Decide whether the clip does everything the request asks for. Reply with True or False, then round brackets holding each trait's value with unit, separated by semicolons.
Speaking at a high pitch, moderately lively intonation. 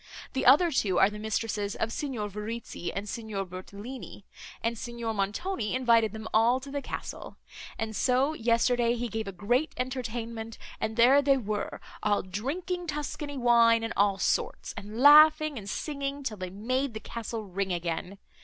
True (230 Hz; 4.0 semitones)